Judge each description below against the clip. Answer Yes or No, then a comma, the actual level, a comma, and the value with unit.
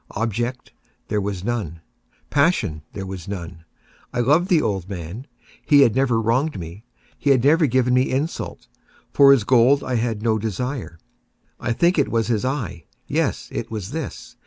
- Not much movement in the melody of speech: No, average, 5.3 semitones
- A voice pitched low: Yes, low, 120 Hz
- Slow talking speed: No, average, 170 wpm